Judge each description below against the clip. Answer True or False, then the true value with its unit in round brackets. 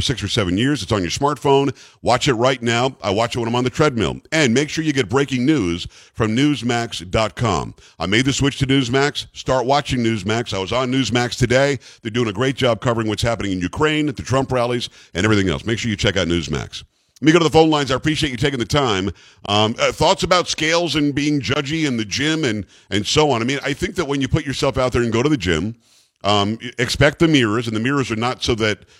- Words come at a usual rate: False (250 wpm)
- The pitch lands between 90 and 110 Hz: False (125 Hz)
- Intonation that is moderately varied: True (4.1 semitones)